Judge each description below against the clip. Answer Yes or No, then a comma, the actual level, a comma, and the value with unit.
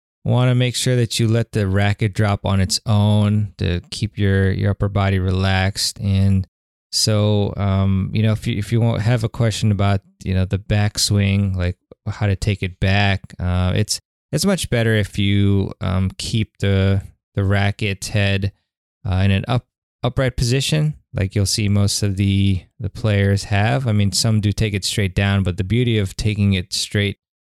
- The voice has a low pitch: Yes, low, 100 Hz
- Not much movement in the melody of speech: Yes, narrow, 2.2 semitones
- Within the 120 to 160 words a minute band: No, average, 190 wpm